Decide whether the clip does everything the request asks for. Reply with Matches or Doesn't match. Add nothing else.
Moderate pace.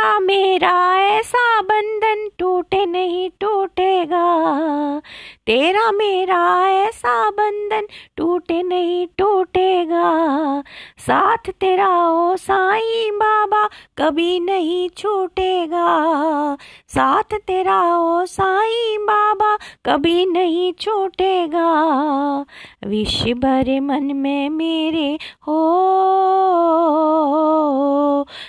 Doesn't match